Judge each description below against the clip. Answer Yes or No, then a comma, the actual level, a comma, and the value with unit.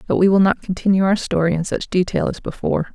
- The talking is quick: Yes, fast, 245 wpm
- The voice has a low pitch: No, medium, 185 Hz